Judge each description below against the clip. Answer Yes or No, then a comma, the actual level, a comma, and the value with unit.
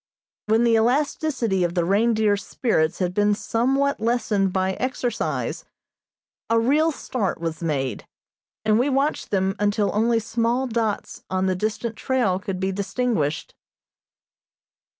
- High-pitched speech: Yes, high, 215 Hz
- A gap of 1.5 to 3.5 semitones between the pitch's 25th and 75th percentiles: No, average, 4.1 semitones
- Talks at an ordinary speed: No, slow, 130 wpm